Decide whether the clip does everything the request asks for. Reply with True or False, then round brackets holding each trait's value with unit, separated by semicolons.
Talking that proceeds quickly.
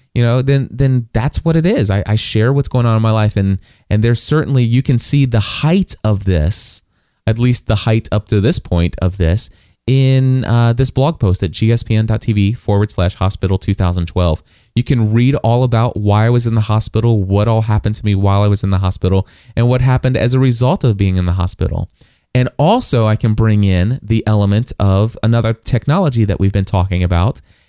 True (210 wpm)